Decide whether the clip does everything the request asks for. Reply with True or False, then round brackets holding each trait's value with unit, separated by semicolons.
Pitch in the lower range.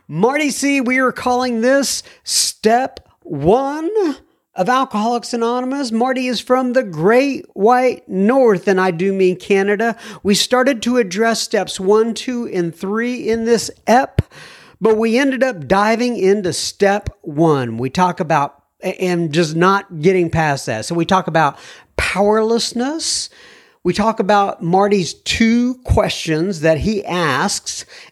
False (220 Hz)